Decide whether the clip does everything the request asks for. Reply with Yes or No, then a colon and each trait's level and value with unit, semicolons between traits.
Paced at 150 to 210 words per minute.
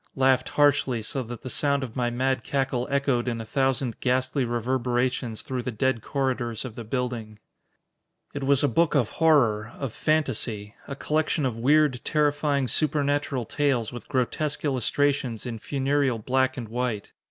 Yes: average, 160 wpm